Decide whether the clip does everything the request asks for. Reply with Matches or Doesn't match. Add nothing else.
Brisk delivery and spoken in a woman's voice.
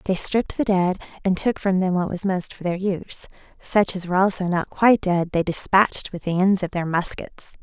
Matches